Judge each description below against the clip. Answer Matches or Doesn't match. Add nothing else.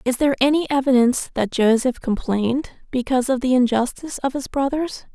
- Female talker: Matches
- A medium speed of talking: Matches